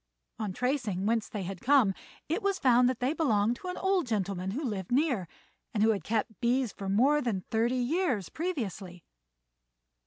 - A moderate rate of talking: Yes, average, 180 wpm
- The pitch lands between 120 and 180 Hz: No, high, 235 Hz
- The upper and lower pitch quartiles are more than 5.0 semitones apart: Yes, wide, 5.6 semitones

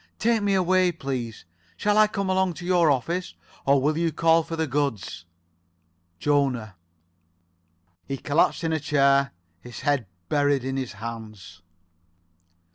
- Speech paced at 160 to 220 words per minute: No, average, 140 wpm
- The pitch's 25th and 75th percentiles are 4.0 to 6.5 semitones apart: Yes, average, 5.2 semitones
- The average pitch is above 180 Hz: No, medium, 145 Hz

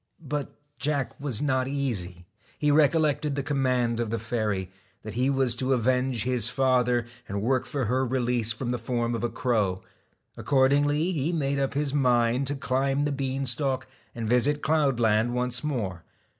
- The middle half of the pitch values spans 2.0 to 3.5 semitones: Yes, average, 2.9 semitones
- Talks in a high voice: No, low, 130 Hz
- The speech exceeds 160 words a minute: Yes, average, 170 wpm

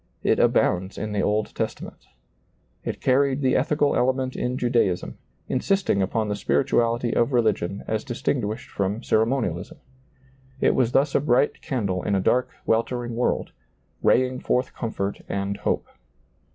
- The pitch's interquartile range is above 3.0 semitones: Yes, average, 4.0 semitones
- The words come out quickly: No, average, 140 wpm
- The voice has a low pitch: Yes, low, 120 Hz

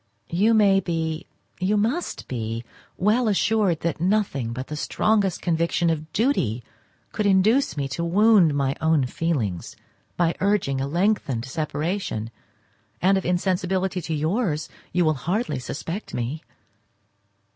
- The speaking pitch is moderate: Yes, medium, 170 Hz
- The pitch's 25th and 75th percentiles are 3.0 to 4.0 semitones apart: No, wide, 5.5 semitones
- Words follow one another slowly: Yes, slow, 125 wpm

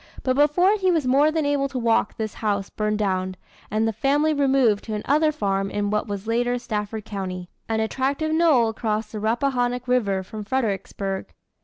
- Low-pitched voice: No, high, 225 Hz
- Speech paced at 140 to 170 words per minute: No, average, 180 wpm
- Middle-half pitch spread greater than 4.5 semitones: Yes, average, 4.9 semitones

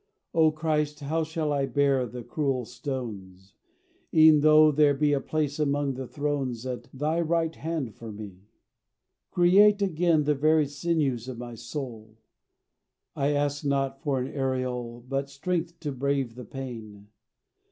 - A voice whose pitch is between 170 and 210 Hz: No, medium, 140 Hz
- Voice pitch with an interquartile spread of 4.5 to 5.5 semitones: No, average, 3.6 semitones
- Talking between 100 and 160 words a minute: Yes, average, 150 wpm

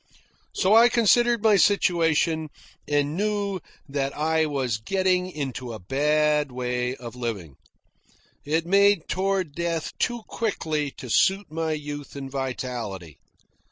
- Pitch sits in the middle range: Yes, medium, 155 Hz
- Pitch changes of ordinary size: No, wide, 6.0 semitones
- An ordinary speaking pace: No, slow, 125 wpm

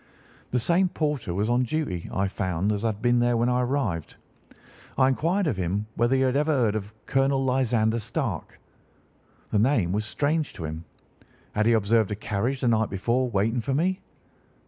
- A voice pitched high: No, low, 120 Hz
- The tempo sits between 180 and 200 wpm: Yes, average, 185 wpm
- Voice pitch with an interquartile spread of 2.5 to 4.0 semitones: No, average, 4.4 semitones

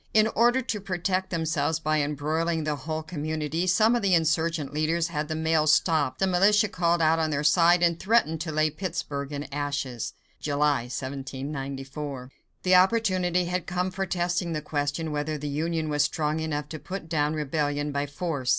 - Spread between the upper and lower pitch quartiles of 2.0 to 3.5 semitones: Yes, average, 3.2 semitones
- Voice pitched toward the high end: No, medium, 155 Hz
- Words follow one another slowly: No, average, 180 wpm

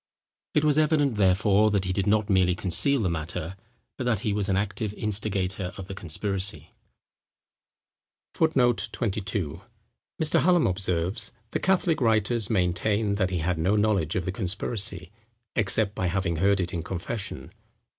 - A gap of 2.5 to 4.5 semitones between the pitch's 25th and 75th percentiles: Yes, average, 2.8 semitones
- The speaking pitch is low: Yes, low, 100 Hz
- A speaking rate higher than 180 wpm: No, average, 155 wpm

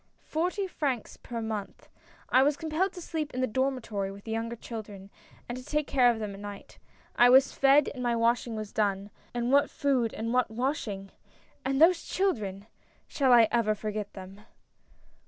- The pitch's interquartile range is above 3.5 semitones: Yes, average, 4.4 semitones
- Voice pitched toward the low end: No, high, 240 Hz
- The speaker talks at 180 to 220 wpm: Yes, average, 190 wpm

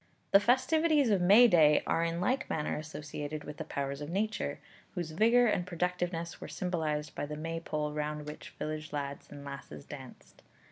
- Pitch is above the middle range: No, medium, 160 Hz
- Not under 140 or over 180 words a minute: Yes, average, 175 wpm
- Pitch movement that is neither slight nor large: Yes, average, 3.9 semitones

